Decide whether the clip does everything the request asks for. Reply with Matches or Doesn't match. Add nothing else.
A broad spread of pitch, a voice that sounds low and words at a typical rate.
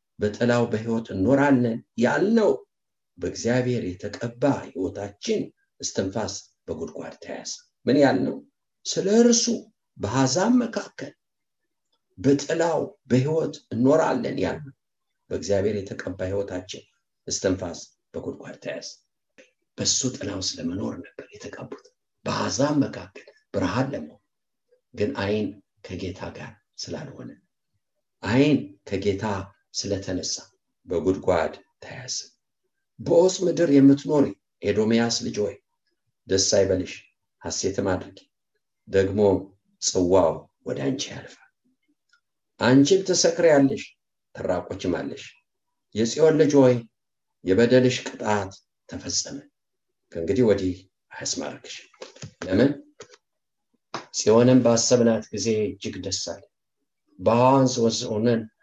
Doesn't match